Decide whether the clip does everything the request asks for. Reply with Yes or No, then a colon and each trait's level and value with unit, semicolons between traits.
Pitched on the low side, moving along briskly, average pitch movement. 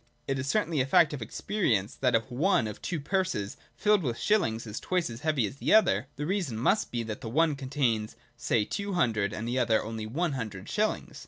No: low, 130 Hz; fast, 220 wpm; wide, 7.2 semitones